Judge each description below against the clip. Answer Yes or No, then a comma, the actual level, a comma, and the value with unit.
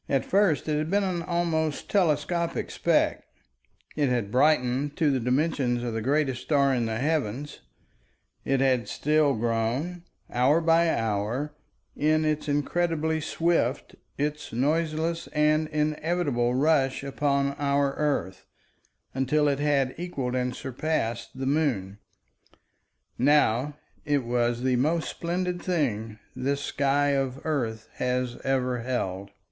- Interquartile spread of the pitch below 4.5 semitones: Yes, average, 3.8 semitones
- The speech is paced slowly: Yes, slow, 130 wpm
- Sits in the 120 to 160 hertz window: Yes, medium, 140 Hz